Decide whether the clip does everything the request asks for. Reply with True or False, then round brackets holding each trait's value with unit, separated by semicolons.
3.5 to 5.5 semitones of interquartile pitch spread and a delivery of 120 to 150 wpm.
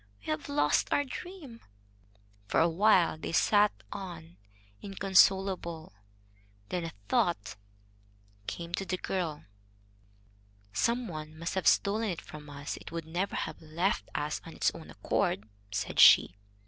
True (4.0 semitones; 140 wpm)